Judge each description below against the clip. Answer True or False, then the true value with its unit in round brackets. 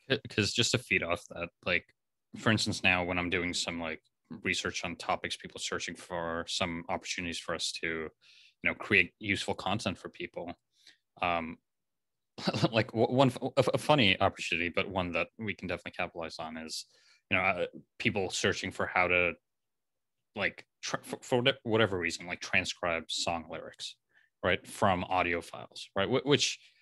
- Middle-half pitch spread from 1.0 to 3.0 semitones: False (4.4 semitones)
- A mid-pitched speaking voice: False (95 Hz)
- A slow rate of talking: False (160 wpm)